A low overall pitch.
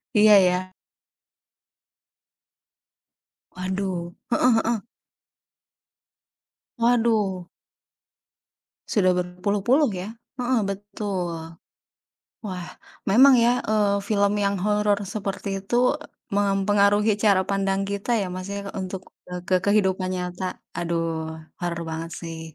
No: high, 195 Hz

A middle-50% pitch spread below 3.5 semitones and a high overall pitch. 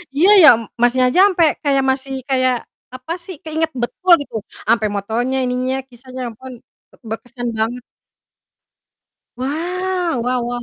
No: average, 4.4 semitones; very high, 260 Hz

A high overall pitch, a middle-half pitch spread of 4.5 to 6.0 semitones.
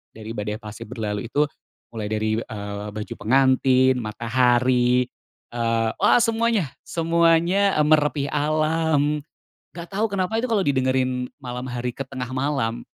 No: low, 130 Hz; average, 5.2 semitones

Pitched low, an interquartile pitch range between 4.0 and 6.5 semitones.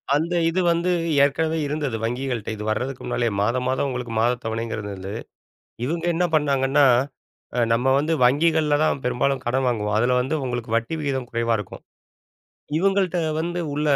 Yes: low, 130 Hz; average, 4.6 semitones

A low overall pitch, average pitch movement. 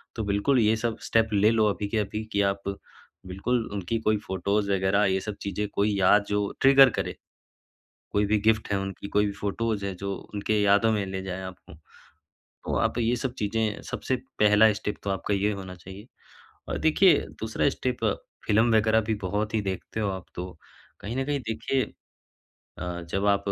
No: low, 105 Hz; narrow, 2.2 semitones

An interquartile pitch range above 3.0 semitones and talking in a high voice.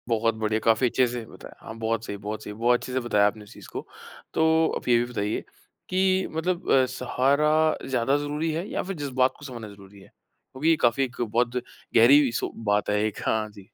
No: average, 4.6 semitones; low, 120 Hz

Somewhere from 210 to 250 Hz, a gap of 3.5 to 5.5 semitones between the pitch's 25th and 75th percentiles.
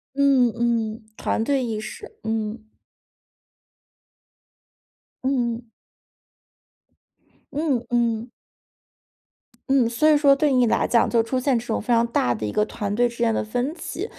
No: high, 235 Hz; average, 2.7 semitones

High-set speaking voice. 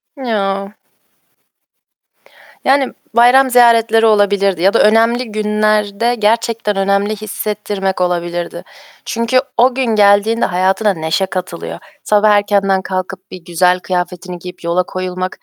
Yes: high, 200 Hz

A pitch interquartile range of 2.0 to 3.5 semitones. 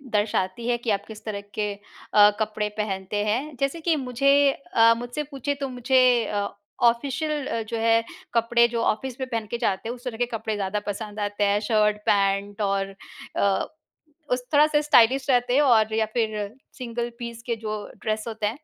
Yes: average, 3.0 semitones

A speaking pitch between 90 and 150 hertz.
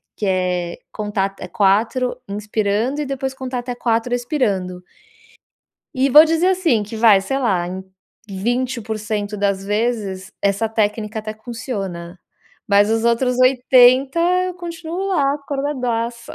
No: high, 230 Hz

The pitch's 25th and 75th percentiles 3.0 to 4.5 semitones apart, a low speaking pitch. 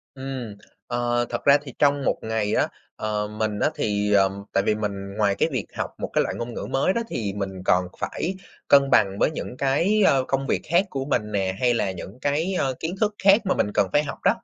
No: wide, 5.6 semitones; low, 120 Hz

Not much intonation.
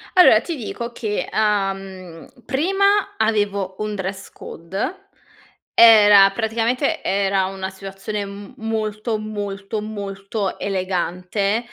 Yes: narrow, 2.3 semitones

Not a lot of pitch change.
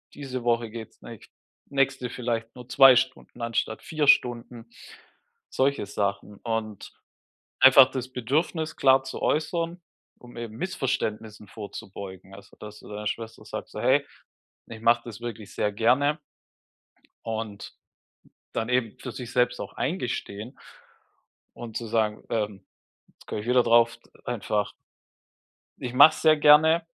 No: average, 3.2 semitones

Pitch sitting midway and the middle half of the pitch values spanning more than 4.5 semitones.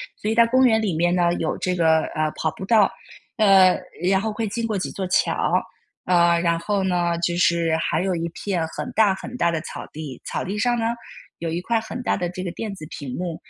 No: medium, 180 Hz; average, 3.8 semitones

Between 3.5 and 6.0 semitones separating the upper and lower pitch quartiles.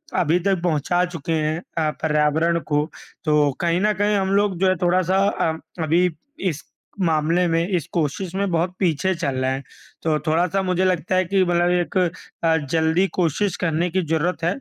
No: narrow, 2.6 semitones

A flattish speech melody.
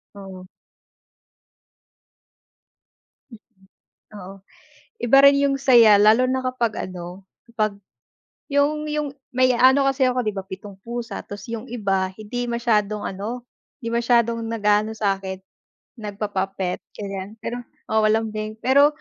No: average, 3.6 semitones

